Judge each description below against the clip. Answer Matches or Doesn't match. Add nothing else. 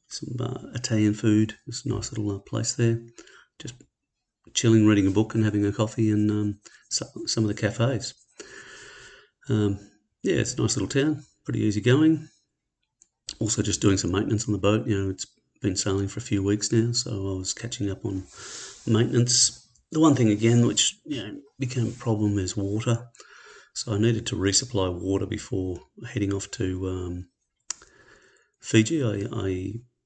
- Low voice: Matches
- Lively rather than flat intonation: Doesn't match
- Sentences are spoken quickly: Doesn't match